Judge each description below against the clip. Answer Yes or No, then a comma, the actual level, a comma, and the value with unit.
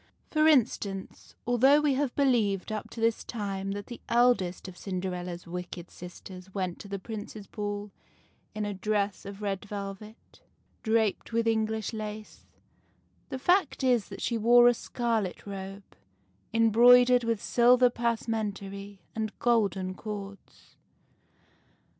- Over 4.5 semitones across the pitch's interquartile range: No, average, 3.2 semitones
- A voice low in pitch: No, high, 215 Hz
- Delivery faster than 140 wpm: No, slow, 135 wpm